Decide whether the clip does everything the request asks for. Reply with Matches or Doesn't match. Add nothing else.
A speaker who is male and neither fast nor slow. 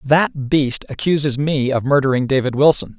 Matches